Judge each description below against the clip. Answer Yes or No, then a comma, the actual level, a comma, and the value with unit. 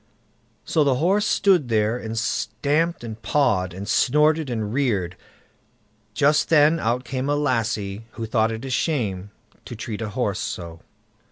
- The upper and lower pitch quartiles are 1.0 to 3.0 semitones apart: No, average, 5.2 semitones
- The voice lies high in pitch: No, low, 120 Hz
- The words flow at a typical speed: Yes, average, 155 wpm